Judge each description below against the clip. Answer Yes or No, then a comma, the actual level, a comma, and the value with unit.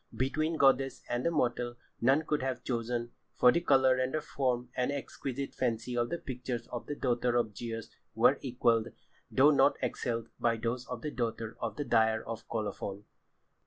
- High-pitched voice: No, low, 125 Hz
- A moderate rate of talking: Yes, average, 170 wpm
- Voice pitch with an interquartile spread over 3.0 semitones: No, narrow, 2.4 semitones